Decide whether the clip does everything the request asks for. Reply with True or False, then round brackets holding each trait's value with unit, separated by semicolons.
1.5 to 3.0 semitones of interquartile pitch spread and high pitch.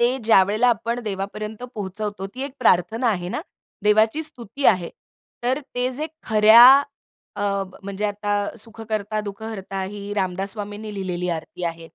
True (2.7 semitones; 210 Hz)